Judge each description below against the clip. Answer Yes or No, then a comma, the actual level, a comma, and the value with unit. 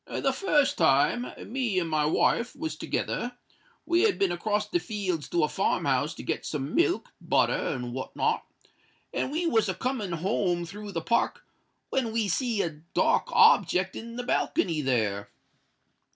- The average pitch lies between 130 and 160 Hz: No, high, 200 Hz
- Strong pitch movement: Yes, wide, 7.2 semitones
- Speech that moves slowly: No, average, 170 wpm